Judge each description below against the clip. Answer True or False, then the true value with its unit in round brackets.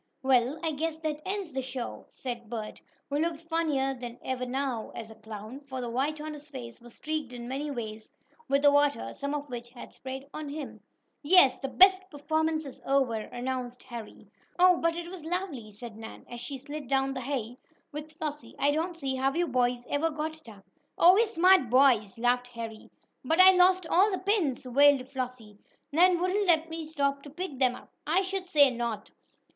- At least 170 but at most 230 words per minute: True (200 wpm)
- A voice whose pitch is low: False (275 Hz)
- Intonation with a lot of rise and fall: False (4.4 semitones)